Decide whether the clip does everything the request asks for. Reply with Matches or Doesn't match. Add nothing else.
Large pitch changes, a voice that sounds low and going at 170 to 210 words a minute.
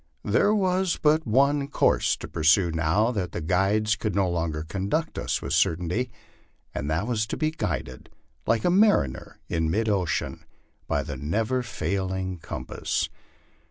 Doesn't match